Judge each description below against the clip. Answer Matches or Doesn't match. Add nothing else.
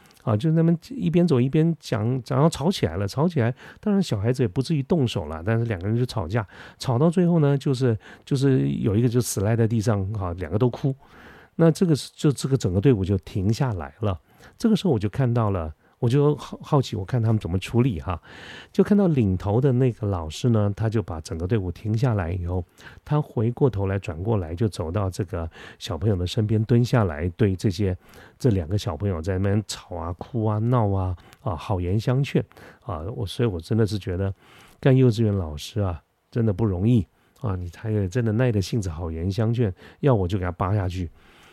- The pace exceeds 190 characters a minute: Matches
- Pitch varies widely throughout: Doesn't match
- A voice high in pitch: Doesn't match